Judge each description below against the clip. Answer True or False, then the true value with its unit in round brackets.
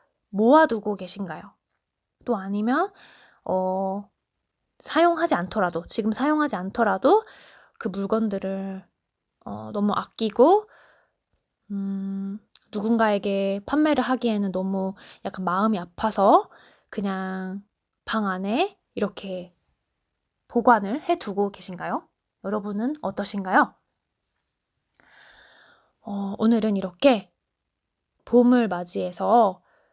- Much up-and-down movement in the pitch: False (3.8 semitones)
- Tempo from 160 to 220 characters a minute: True (210 characters per minute)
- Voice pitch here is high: True (205 Hz)